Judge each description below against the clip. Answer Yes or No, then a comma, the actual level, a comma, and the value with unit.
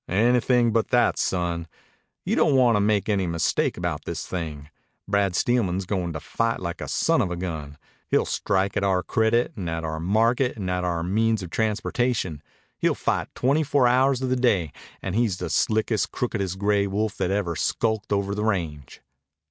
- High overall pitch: No, low, 100 Hz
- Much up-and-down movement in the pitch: No, average, 4.6 semitones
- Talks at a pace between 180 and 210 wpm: Yes, average, 190 wpm